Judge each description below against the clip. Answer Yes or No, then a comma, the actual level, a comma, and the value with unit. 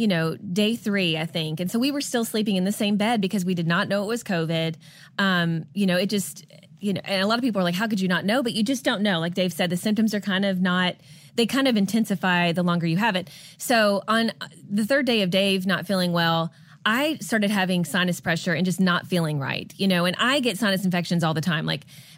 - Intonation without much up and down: No, average, 3.8 semitones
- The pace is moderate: No, fast, 260 wpm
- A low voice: No, high, 190 Hz